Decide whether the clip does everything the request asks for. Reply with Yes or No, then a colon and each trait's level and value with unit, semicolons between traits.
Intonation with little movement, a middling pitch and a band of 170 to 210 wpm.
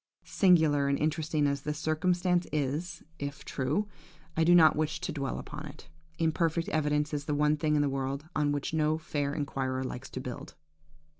Yes: narrow, 2.1 semitones; medium, 150 Hz; average, 180 wpm